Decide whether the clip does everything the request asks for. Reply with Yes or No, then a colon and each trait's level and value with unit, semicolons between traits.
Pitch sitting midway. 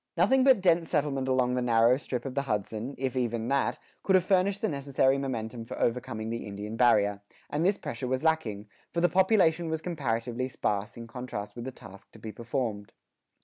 No: low, 130 Hz